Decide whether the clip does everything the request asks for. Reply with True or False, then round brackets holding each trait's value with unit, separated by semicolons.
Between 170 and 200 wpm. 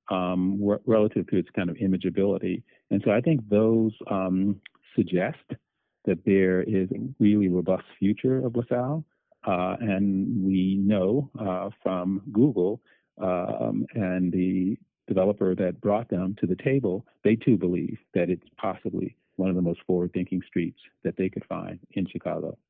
False (155 wpm)